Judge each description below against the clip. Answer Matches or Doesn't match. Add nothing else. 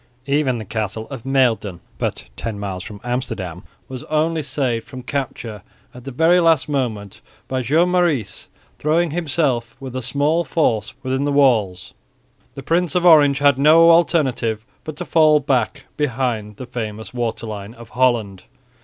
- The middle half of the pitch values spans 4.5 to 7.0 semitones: Matches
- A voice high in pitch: Doesn't match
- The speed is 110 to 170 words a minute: Matches